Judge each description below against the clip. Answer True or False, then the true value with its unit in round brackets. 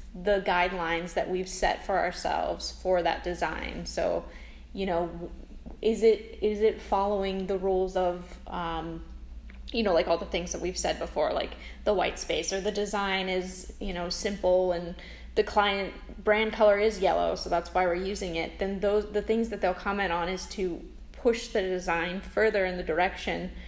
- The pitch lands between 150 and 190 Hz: True (185 Hz)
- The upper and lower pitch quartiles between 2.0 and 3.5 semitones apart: True (2.9 semitones)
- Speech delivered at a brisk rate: False (185 wpm)